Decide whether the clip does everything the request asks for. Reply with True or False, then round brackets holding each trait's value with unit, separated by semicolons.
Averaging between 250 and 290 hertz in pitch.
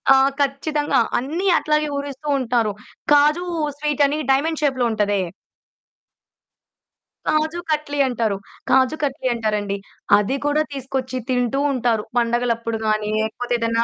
True (260 Hz)